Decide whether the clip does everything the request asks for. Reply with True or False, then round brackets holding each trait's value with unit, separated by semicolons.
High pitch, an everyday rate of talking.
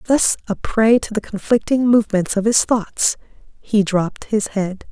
True (215 Hz; 170 wpm)